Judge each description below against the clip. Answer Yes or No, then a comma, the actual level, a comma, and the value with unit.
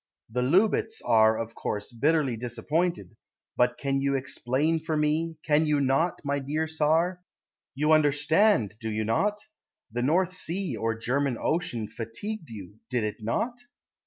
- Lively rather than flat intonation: Yes, wide, 5.9 semitones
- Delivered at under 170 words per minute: Yes, average, 150 wpm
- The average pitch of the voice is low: No, medium, 145 Hz